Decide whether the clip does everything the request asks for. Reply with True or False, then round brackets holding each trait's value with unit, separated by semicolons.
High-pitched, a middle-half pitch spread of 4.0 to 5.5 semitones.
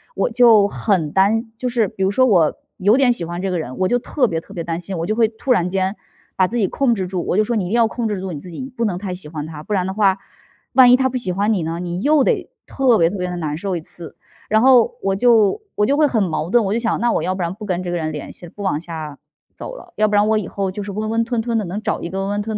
True (200 Hz; 4.4 semitones)